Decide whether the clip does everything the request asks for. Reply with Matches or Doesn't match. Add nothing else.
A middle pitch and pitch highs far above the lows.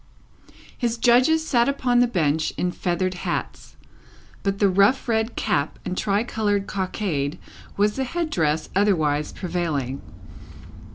Doesn't match